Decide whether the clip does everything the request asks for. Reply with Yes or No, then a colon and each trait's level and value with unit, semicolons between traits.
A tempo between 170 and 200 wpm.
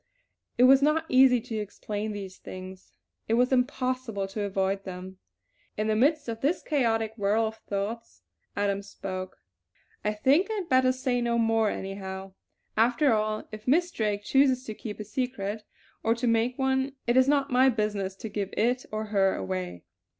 Yes: average, 175 wpm